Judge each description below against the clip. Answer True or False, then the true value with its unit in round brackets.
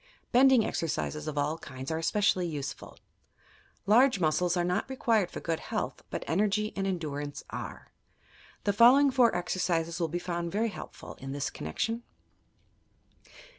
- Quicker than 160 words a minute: False (145 wpm)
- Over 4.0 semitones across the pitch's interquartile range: True (5.2 semitones)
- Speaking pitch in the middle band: True (175 Hz)